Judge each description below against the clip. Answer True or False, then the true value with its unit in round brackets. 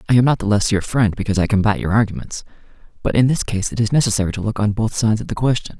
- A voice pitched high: False (110 Hz)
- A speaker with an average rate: False (280 wpm)